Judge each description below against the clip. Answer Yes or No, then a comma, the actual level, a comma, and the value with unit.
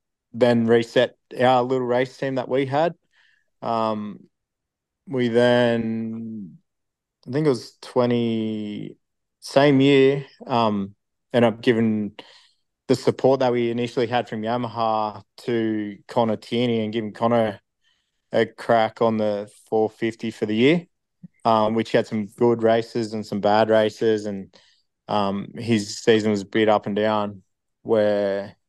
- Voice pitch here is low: Yes, low, 115 Hz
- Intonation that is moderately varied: No, narrow, 2.3 semitones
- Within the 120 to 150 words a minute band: Yes, average, 140 wpm